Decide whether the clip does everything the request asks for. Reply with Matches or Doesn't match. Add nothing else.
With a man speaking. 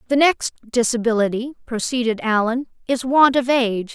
Doesn't match